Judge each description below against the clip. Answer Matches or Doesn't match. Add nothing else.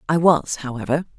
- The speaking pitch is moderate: Matches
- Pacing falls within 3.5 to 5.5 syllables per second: Doesn't match